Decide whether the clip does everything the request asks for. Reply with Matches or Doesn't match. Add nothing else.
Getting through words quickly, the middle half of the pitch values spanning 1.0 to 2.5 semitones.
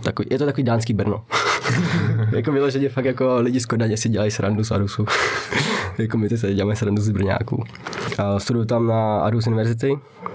Doesn't match